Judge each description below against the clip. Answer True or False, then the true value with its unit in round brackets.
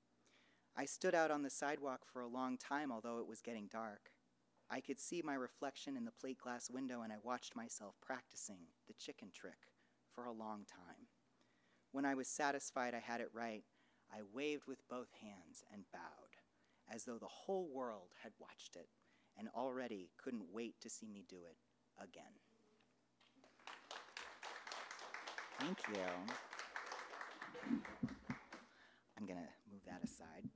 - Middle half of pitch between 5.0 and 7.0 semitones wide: True (5.4 semitones)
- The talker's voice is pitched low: True (120 Hz)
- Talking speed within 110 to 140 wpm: False (155 wpm)